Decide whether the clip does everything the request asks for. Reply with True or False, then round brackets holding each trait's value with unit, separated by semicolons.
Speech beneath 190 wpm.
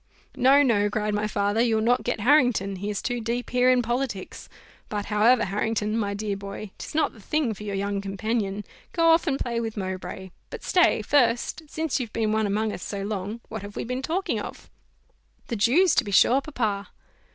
False (205 wpm)